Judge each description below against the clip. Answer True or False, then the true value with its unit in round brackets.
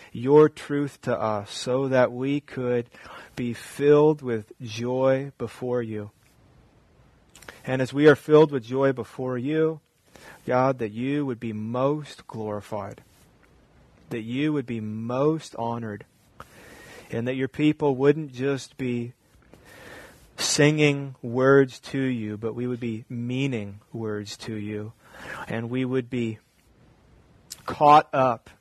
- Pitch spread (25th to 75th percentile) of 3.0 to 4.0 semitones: True (3.3 semitones)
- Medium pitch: False (125 Hz)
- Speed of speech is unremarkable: False (130 wpm)